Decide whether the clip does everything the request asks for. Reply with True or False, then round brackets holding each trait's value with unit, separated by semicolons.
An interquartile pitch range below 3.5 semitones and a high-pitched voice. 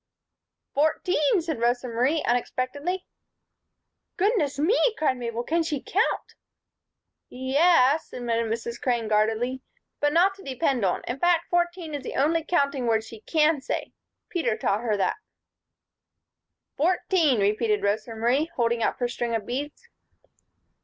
False (5.6 semitones; 265 Hz)